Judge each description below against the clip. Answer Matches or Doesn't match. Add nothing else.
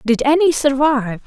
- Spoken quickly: Doesn't match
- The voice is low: Doesn't match